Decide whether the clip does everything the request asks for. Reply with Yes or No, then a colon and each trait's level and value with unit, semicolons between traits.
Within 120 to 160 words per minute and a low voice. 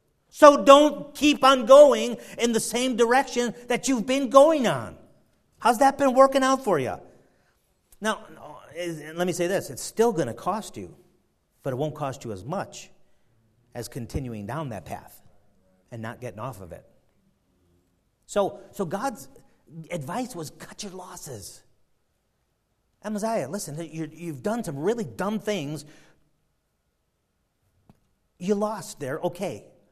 No: average, 140 wpm; medium, 175 Hz